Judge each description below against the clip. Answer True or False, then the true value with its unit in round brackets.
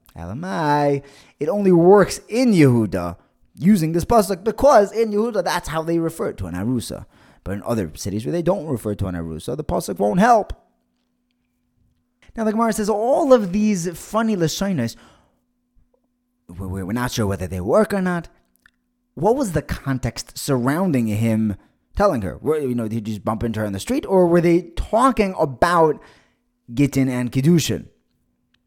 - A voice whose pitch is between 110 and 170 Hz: True (140 Hz)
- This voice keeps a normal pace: True (170 wpm)